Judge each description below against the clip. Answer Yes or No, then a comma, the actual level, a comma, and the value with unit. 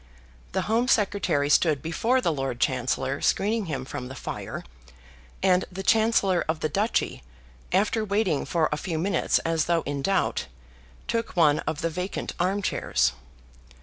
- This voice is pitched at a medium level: Yes, medium, 170 Hz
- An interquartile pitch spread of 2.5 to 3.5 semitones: No, wide, 5.5 semitones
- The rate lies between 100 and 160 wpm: Yes, average, 150 wpm